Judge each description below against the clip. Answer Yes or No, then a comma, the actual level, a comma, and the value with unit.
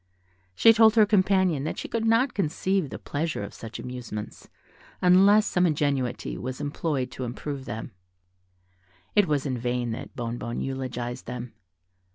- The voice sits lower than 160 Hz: Yes, medium, 140 Hz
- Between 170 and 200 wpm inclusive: No, average, 150 wpm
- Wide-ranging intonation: Yes, wide, 7.3 semitones